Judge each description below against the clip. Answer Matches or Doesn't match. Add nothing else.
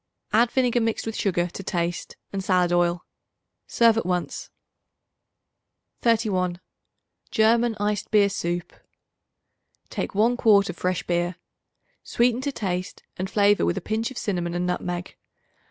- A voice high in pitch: Matches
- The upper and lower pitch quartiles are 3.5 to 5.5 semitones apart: Matches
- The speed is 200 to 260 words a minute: Doesn't match